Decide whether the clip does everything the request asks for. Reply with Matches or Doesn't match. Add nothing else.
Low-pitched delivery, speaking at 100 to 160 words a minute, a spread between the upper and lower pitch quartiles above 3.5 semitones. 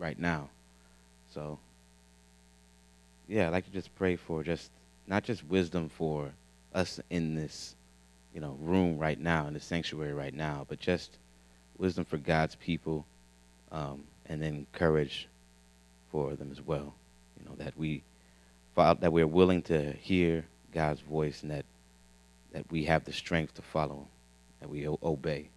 Matches